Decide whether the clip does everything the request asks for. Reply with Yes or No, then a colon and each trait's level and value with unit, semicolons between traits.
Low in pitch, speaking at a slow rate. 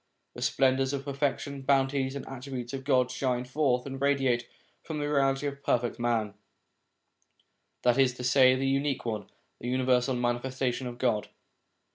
No: low, 130 Hz; average, 170 wpm